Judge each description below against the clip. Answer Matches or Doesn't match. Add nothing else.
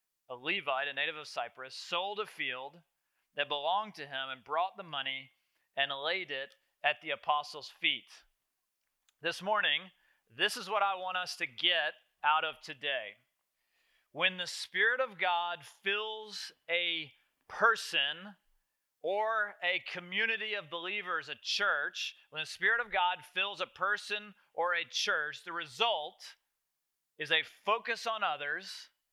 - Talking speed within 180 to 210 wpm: Doesn't match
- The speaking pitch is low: Doesn't match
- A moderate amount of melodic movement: Doesn't match